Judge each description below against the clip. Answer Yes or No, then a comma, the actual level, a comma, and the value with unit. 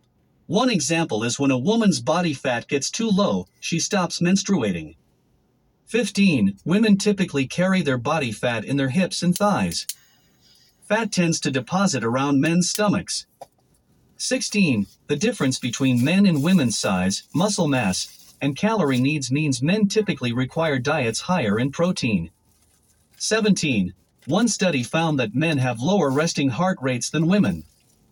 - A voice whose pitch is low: No, medium, 155 Hz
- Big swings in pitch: Yes, wide, 7.2 semitones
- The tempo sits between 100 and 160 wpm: Yes, average, 145 wpm